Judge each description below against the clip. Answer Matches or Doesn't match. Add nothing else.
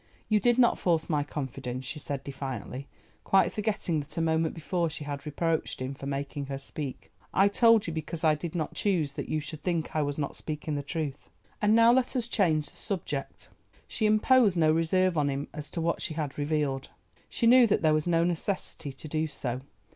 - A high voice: Doesn't match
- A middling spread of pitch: Matches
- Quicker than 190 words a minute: Matches